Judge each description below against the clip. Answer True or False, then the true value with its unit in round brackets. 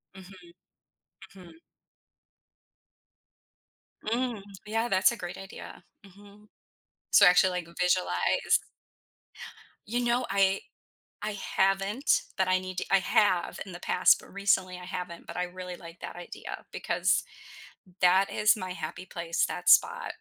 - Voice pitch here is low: False (185 Hz)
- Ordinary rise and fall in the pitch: False (2.1 semitones)